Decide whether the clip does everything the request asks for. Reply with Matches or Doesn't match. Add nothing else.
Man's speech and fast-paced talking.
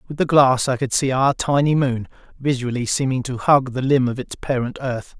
Matches